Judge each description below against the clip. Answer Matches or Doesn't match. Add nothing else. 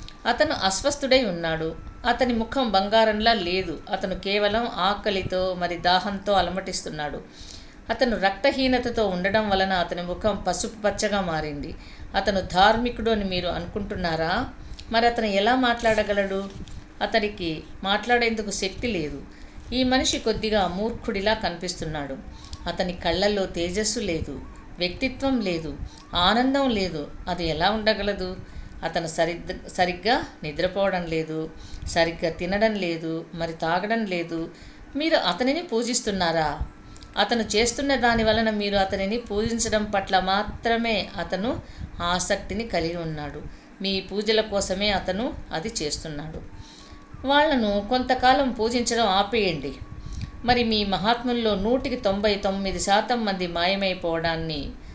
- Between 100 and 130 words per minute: Matches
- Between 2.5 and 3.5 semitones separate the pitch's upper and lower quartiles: Doesn't match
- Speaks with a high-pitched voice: Matches